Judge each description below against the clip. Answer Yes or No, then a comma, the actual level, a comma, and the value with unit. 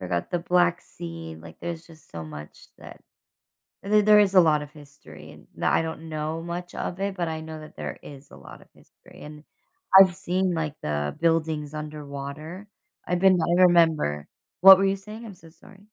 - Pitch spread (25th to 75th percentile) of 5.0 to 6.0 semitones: No, average, 3.5 semitones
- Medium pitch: Yes, medium, 160 Hz